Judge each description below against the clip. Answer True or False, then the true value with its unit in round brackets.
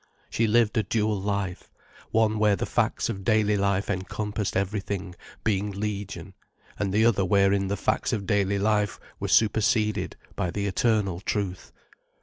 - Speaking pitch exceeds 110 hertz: False (100 Hz)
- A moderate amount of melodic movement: False (1.5 semitones)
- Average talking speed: True (150 wpm)